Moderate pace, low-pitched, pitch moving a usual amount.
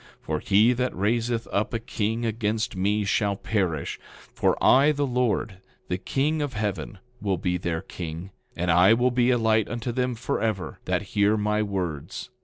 Yes: average, 180 wpm; low, 105 Hz; average, 4.0 semitones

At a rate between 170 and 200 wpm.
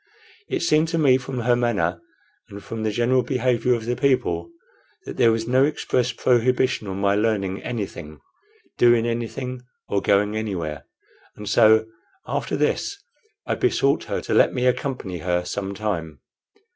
No: average, 160 wpm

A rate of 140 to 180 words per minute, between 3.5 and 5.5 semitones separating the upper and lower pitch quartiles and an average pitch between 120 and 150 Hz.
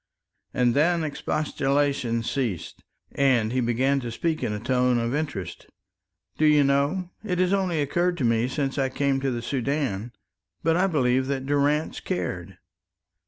Yes: average, 160 wpm; average, 3.9 semitones; low, 135 Hz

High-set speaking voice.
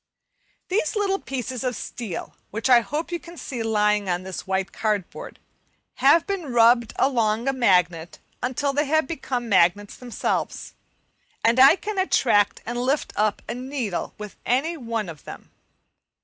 Yes: high, 240 Hz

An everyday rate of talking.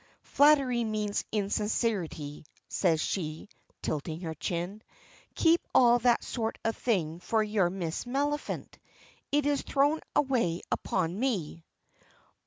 No: slow, 115 wpm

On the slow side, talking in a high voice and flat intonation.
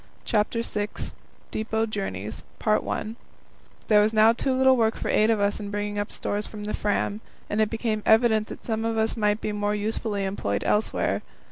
No: average, 180 wpm; high, 215 Hz; narrow, 1.3 semitones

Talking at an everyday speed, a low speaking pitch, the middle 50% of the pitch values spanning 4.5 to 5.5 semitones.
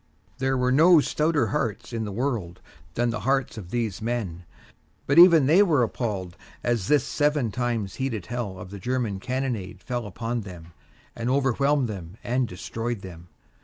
Yes: average, 170 wpm; low, 120 Hz; average, 4.9 semitones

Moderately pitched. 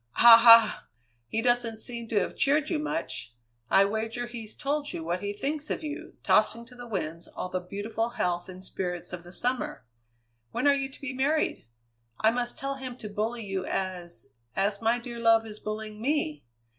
No: high, 225 Hz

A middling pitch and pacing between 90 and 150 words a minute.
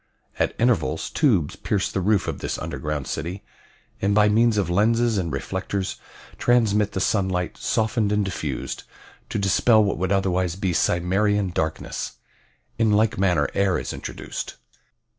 No: low, 100 Hz; average, 145 wpm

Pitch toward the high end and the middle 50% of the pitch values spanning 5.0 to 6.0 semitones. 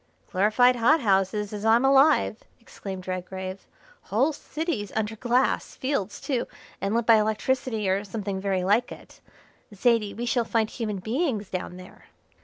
No: high, 215 Hz; average, 3.7 semitones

